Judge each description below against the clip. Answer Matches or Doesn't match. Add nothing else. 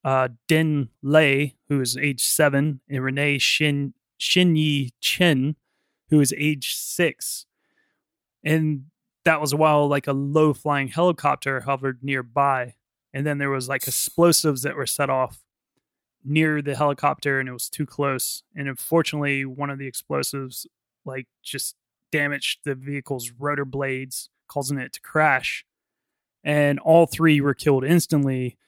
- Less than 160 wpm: Matches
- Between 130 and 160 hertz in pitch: Matches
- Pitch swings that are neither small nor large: Doesn't match